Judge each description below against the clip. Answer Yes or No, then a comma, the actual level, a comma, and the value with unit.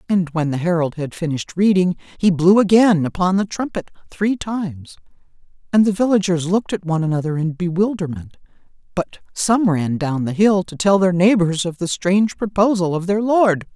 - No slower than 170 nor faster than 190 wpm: Yes, average, 175 wpm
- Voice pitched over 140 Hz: Yes, medium, 185 Hz